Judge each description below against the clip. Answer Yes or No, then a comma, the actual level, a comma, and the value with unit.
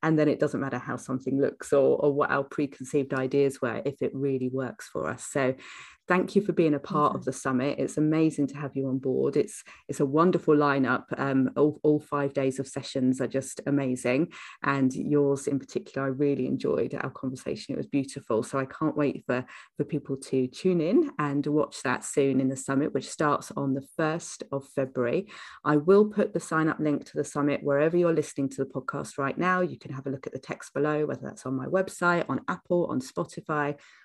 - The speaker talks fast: Yes, fast, 220 wpm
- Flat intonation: Yes, narrow, 2.1 semitones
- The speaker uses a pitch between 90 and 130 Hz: No, medium, 140 Hz